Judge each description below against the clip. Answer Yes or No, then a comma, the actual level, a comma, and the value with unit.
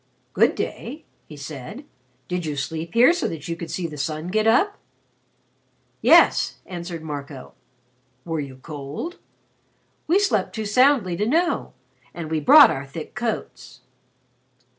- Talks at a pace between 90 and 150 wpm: Yes, average, 140 wpm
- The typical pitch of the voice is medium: Yes, medium, 170 Hz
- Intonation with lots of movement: Yes, wide, 7.9 semitones